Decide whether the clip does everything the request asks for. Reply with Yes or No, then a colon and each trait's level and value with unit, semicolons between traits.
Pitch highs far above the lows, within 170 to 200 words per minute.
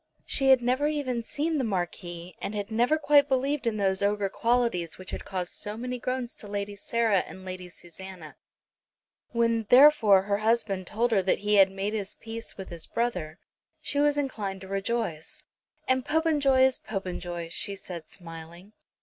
No: average, 5.0 semitones; average, 175 wpm